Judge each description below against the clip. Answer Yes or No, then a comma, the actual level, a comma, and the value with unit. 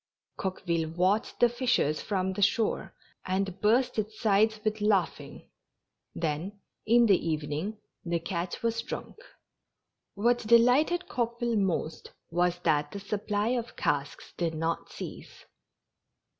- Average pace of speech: No, slow, 125 wpm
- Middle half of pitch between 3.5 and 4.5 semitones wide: No, average, 5.0 semitones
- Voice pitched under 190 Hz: No, high, 200 Hz